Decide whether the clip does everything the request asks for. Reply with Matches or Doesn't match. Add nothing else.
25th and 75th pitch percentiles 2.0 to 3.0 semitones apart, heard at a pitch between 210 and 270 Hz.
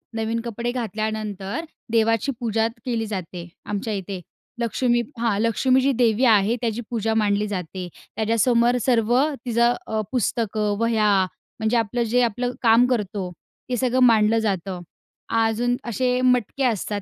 Matches